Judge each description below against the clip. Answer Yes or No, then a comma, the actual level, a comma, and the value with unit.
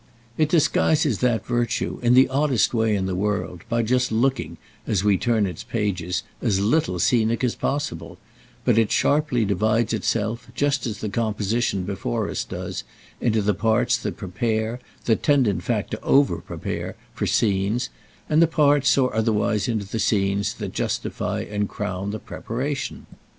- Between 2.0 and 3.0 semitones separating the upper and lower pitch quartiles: No, average, 3.6 semitones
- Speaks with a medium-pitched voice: No, low, 110 Hz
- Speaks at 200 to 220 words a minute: No, average, 165 wpm